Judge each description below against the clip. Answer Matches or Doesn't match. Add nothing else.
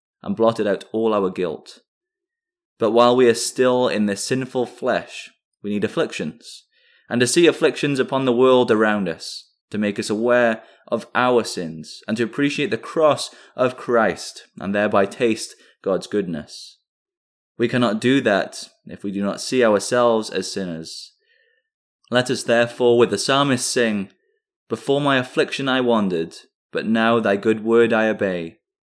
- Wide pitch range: Doesn't match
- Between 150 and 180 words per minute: Matches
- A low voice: Matches